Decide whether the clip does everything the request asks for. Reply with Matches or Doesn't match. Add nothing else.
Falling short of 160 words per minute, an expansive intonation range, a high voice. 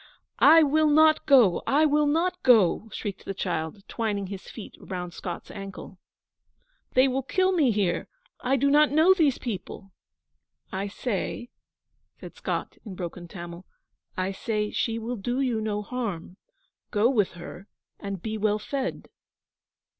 Matches